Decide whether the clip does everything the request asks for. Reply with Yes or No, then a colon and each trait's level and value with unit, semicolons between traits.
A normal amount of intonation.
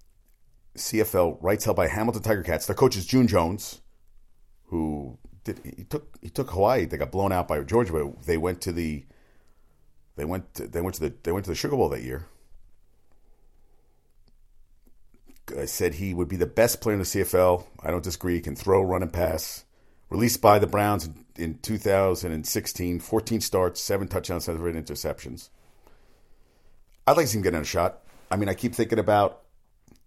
Yes: average, 4.5 semitones